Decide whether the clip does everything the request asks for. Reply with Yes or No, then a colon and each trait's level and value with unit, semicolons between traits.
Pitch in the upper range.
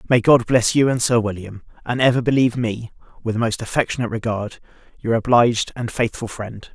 No: low, 115 Hz